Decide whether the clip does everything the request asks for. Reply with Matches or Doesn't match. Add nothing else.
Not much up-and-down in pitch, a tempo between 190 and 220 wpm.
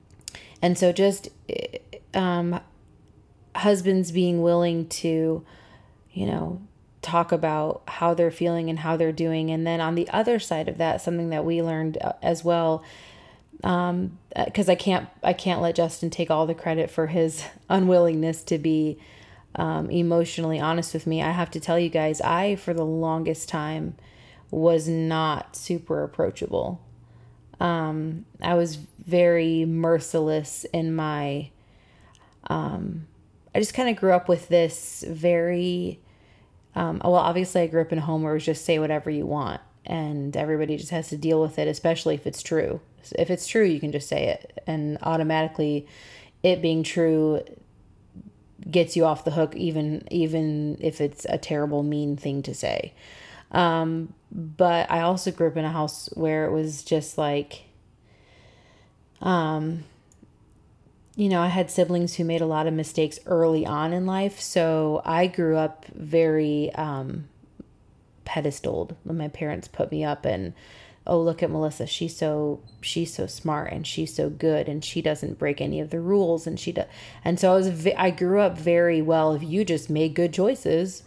Doesn't match